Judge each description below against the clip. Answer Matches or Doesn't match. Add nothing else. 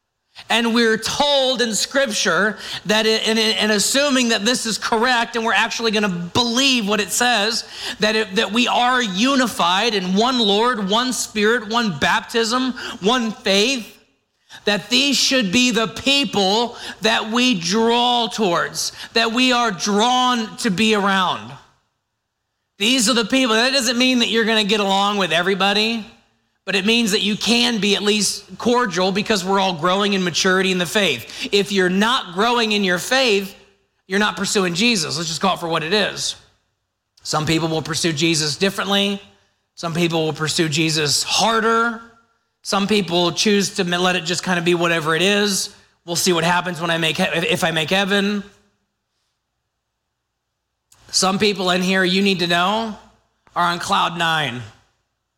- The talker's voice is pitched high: Matches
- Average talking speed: Matches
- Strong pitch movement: Doesn't match